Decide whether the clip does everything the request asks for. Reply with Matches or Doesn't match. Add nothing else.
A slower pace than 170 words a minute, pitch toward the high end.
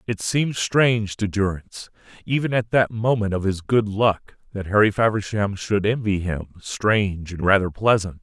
Doesn't match